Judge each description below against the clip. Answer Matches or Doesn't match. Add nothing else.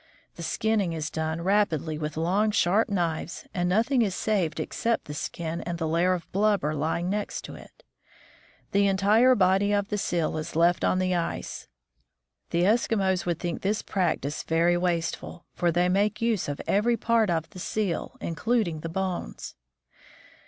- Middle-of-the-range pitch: Matches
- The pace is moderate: Matches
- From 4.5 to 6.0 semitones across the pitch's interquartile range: Doesn't match